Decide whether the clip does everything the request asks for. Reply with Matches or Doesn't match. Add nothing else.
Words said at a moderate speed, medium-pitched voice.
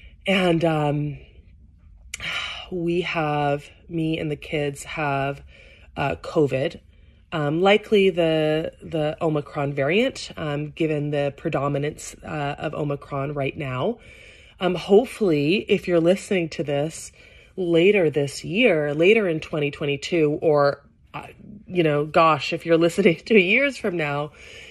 Doesn't match